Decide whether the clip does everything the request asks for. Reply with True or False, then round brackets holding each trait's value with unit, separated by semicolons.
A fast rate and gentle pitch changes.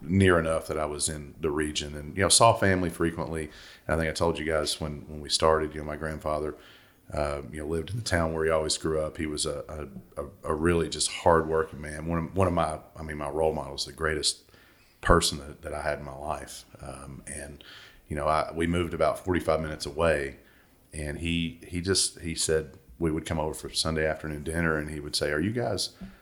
True (235 wpm; 1.6 semitones)